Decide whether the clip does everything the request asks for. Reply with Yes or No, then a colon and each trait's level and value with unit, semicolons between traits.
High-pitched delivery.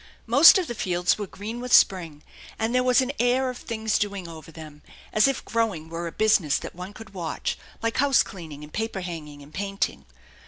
Yes: high, 200 Hz